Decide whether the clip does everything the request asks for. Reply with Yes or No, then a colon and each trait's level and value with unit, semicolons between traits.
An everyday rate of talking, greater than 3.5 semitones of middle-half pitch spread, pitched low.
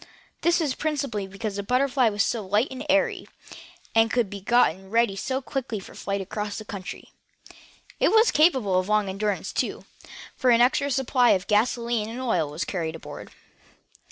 No: average, 180 wpm; average, 4.5 semitones; high, 225 Hz